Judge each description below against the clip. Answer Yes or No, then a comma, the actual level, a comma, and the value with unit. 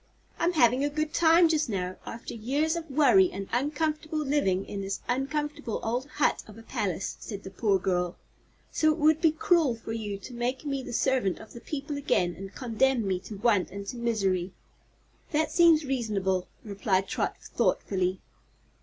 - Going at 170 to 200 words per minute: Yes, average, 175 wpm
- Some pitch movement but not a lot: No, wide, 7.2 semitones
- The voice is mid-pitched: No, high, 240 Hz